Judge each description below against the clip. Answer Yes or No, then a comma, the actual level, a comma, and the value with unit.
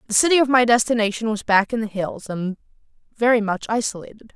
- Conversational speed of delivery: Yes, average, 195 wpm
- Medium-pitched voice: No, high, 220 Hz